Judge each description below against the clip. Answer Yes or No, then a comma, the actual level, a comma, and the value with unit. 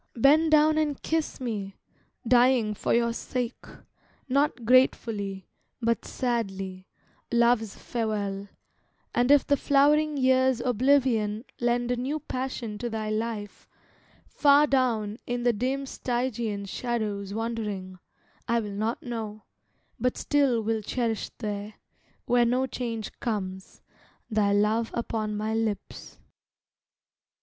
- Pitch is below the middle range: No, high, 235 Hz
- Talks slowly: Yes, slow, 120 wpm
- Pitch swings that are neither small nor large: Yes, average, 3.3 semitones